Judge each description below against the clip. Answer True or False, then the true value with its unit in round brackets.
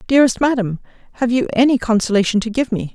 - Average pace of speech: True (185 wpm)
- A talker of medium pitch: False (235 Hz)